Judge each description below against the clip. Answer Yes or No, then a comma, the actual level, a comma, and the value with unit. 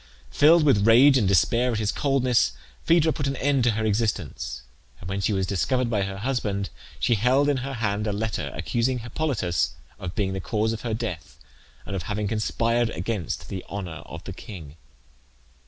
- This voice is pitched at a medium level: No, low, 110 Hz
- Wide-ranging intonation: No, average, 4.3 semitones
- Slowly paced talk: No, average, 190 wpm